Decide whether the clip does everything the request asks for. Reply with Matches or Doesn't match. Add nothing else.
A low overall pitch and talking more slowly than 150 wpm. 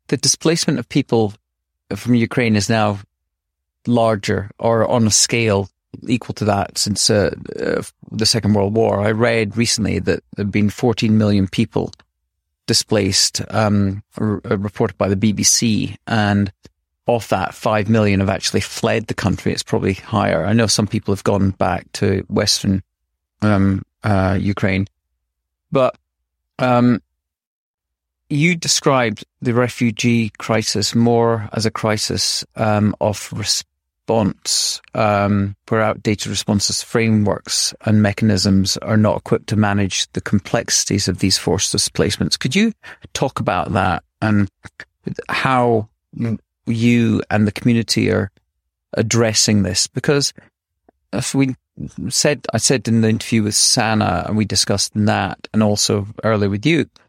Matches